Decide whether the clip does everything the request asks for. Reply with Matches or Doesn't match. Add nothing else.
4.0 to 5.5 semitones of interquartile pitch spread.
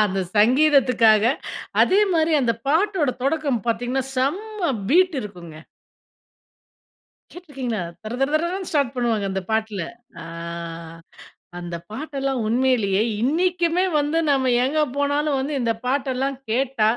Matches